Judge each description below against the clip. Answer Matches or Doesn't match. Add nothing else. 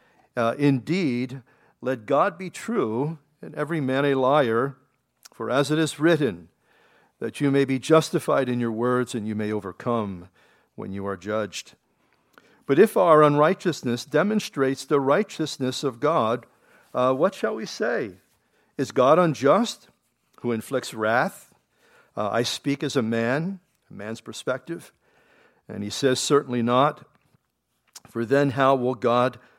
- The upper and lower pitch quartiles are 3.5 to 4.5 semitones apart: Matches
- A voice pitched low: Matches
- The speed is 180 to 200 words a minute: Doesn't match